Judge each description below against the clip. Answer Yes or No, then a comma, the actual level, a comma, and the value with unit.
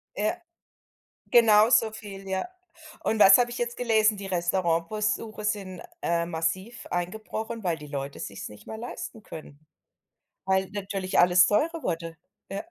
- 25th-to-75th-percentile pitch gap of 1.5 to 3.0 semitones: No, average, 4.0 semitones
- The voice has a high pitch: Yes, high, 195 Hz